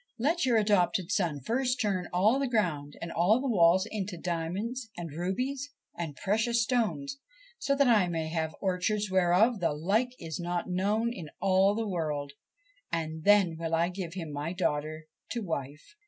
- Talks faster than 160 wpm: Yes, average, 170 wpm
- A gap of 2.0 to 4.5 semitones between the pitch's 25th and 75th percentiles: No, average, 5.1 semitones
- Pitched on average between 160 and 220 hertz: Yes, medium, 185 Hz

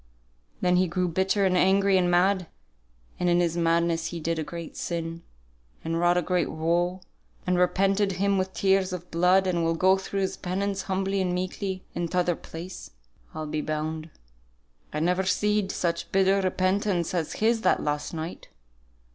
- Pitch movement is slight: Yes, narrow, 2.2 semitones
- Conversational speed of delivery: Yes, average, 175 wpm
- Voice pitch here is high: No, medium, 180 Hz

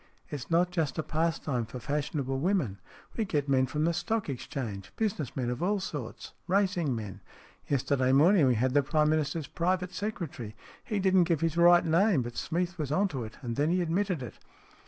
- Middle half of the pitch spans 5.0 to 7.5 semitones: Yes, wide, 5.4 semitones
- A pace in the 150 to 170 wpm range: No, average, 195 wpm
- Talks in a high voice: No, medium, 155 Hz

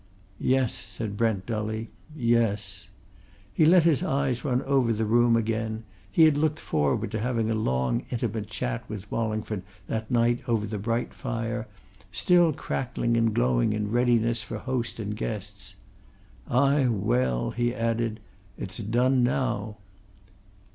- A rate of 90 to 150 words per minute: Yes, average, 140 wpm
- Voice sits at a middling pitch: No, low, 115 Hz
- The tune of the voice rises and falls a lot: No, narrow, 2.5 semitones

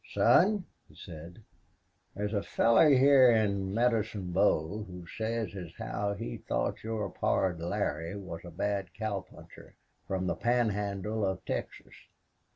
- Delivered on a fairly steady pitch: No, average, 3.2 semitones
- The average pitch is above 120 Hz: No, low, 100 Hz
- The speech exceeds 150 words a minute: No, average, 140 wpm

